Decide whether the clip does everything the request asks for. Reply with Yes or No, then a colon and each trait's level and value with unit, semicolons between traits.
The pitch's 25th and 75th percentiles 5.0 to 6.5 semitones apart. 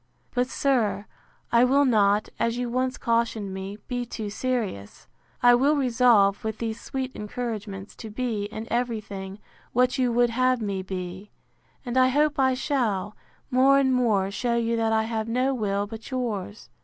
No: average, 3.5 semitones